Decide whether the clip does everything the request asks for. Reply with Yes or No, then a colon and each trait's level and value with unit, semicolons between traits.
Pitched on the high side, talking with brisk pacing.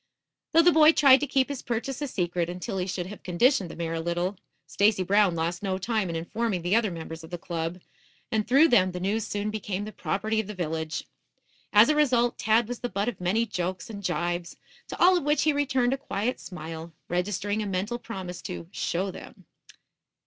Yes: high, 200 Hz; fast, 215 wpm